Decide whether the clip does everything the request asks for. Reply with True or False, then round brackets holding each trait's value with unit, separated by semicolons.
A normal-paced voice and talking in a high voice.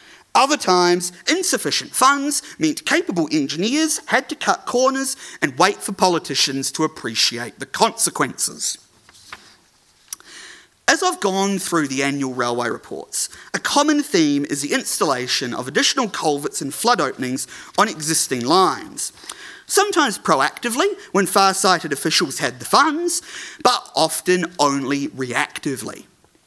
False (120 wpm; 195 Hz)